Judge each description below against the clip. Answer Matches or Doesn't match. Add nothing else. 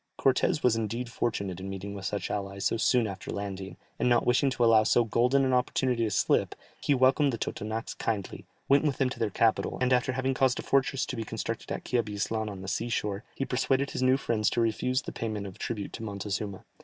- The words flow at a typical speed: Doesn't match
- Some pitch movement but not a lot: Matches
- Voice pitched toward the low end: Matches